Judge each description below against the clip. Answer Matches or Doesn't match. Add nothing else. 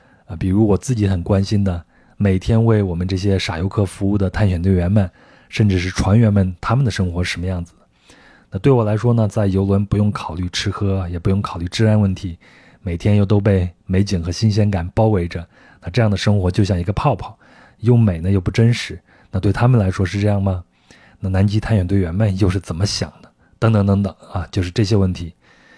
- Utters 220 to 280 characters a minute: Doesn't match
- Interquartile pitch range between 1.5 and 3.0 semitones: Matches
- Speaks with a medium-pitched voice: Doesn't match